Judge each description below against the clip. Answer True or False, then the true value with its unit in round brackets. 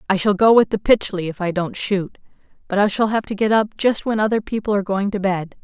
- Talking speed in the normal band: False (265 wpm)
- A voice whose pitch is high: True (200 Hz)